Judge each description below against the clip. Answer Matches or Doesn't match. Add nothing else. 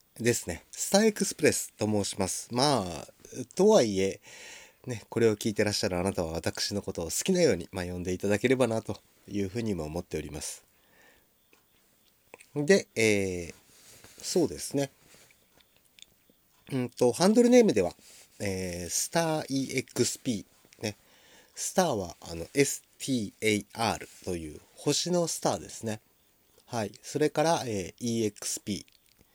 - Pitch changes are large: Matches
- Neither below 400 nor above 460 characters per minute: Doesn't match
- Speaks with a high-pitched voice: Doesn't match